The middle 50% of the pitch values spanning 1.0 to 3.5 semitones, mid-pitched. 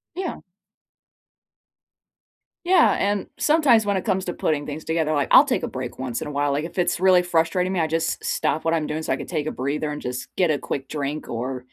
No: average, 4.2 semitones; medium, 160 Hz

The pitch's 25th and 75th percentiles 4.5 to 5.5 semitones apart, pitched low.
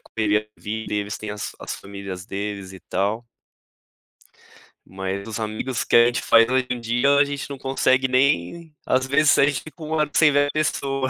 Yes: average, 5.2 semitones; low, 120 Hz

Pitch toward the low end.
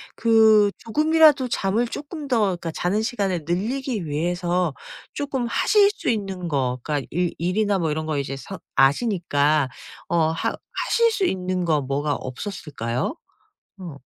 No: medium, 185 Hz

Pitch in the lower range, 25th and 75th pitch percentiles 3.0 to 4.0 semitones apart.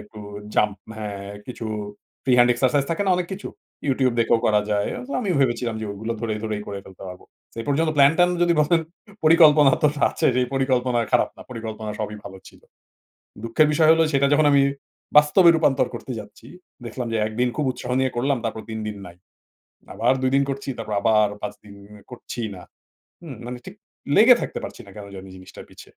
No: low, 125 Hz; average, 4.9 semitones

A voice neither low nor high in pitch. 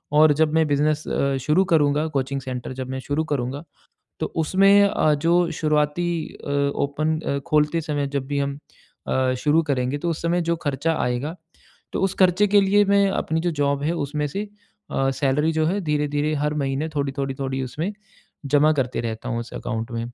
Yes: medium, 150 Hz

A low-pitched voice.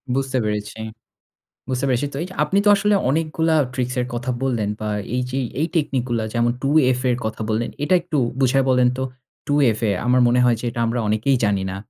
Yes: low, 125 Hz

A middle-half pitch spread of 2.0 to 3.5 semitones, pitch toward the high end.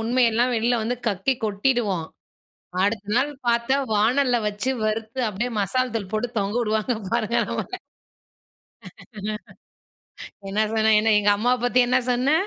Yes: average, 2.7 semitones; high, 230 Hz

